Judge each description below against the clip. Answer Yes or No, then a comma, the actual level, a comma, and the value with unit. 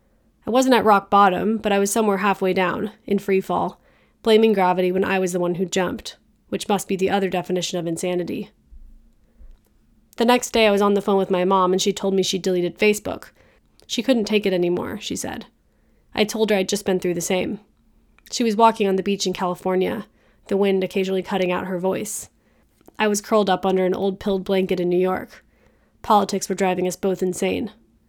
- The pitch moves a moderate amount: No, narrow, 1.8 semitones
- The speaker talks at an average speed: No, fast, 210 wpm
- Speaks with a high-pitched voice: Yes, high, 195 Hz